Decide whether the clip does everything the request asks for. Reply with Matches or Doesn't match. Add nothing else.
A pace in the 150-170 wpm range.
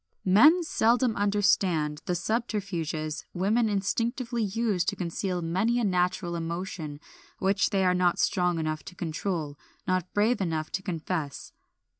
Doesn't match